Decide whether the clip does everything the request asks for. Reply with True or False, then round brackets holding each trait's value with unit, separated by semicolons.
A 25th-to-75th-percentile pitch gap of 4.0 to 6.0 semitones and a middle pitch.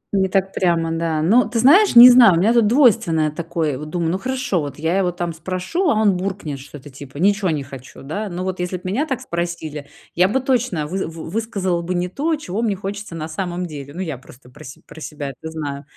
True (4.6 semitones; 180 Hz)